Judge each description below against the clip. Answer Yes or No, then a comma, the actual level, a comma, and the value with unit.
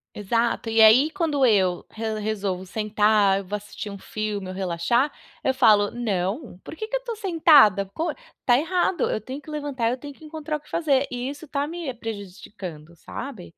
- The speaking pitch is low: No, high, 230 Hz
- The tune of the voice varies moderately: No, wide, 6.5 semitones